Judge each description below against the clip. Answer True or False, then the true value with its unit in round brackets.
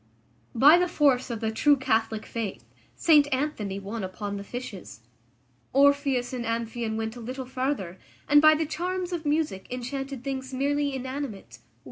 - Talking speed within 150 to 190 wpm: True (155 wpm)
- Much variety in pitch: False (4.4 semitones)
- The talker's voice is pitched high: True (260 Hz)